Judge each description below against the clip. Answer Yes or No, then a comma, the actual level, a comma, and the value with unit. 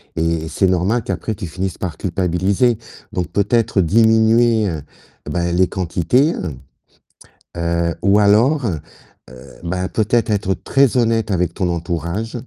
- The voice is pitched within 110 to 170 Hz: No, very low, 95 Hz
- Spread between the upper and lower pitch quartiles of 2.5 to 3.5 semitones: No, average, 4.6 semitones